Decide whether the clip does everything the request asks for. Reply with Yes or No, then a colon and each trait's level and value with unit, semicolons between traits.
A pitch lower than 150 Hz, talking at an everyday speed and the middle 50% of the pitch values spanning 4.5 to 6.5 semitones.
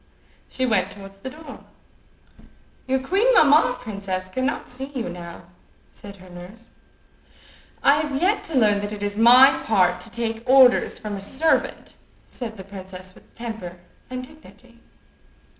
No: high, 230 Hz; average, 150 wpm; average, 5.2 semitones